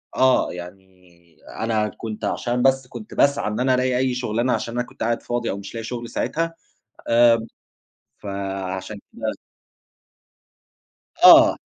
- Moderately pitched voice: No, low, 115 Hz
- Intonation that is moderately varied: Yes, average, 3.0 semitones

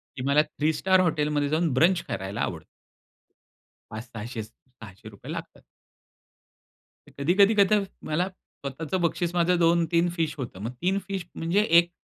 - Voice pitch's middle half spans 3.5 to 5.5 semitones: Yes, average, 4.0 semitones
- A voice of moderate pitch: Yes, medium, 165 Hz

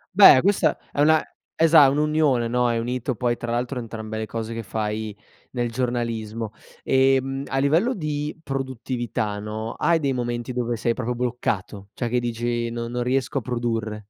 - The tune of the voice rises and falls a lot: No, average, 2.8 semitones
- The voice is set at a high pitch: No, low, 120 Hz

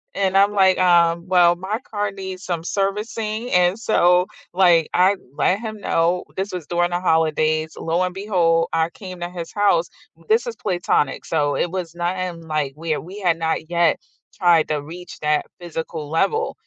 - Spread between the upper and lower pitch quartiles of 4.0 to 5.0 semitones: No, narrow, 2.6 semitones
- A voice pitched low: No, medium, 175 Hz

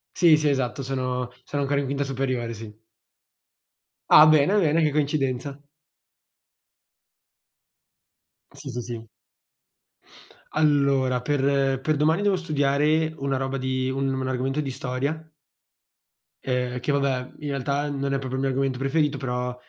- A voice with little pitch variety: Yes, narrow, 2.1 semitones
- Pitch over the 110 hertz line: Yes, low, 135 Hz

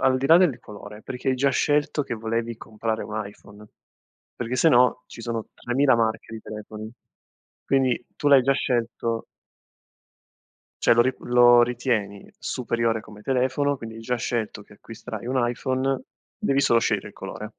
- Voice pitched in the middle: No, low, 120 Hz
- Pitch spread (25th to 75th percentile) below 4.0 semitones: Yes, average, 2.8 semitones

